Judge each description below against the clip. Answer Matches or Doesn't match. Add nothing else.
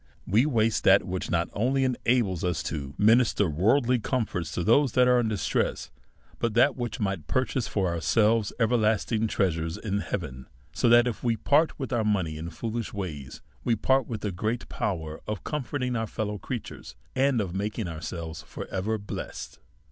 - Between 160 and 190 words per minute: Matches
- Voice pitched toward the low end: Matches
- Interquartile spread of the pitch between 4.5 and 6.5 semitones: Matches